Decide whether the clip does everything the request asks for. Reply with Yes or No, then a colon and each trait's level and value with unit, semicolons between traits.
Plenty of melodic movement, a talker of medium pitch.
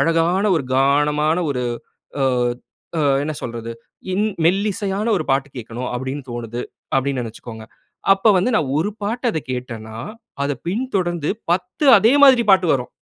Yes: wide, 7.5 semitones; medium, 155 Hz